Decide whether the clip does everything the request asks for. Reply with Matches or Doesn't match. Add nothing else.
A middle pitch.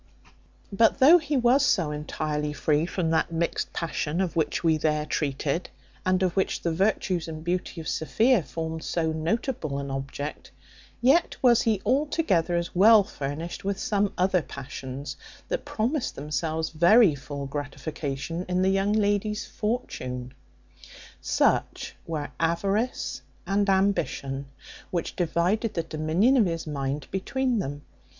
Matches